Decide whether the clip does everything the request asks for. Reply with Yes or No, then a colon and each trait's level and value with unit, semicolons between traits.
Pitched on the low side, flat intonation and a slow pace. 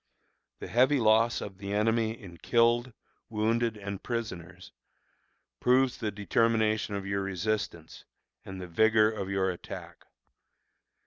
No: low, 110 Hz; average, 3.0 semitones; slow, 125 wpm